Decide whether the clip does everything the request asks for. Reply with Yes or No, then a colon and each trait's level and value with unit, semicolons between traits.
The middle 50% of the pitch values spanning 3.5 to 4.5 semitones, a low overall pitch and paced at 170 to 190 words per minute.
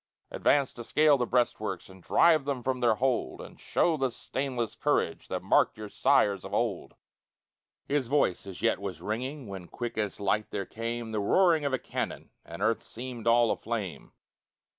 Yes: average, 4.1 semitones; low, 120 Hz; average, 180 wpm